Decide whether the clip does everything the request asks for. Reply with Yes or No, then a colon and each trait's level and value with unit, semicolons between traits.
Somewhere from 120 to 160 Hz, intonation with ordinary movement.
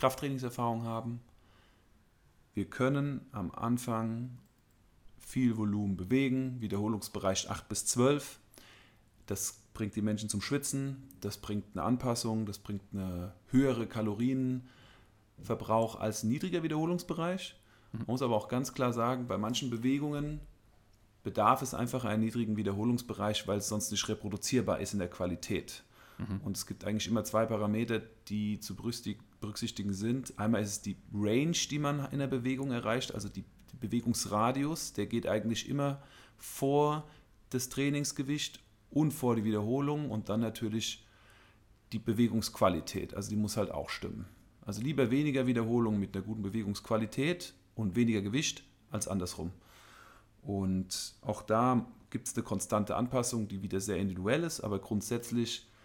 No: low, 110 Hz; average, 3.5 semitones